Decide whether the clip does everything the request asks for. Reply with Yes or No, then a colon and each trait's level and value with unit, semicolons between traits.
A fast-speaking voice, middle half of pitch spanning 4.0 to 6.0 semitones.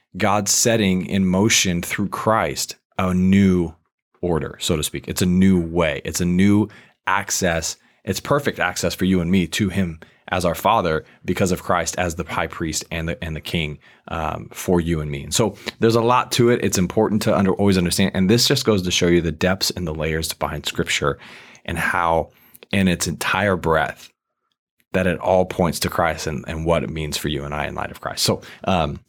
No: fast, 215 wpm; average, 3.0 semitones